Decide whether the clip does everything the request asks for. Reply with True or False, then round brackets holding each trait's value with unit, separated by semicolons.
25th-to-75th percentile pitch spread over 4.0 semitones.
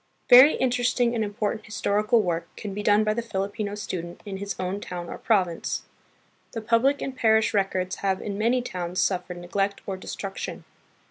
False (3.1 semitones)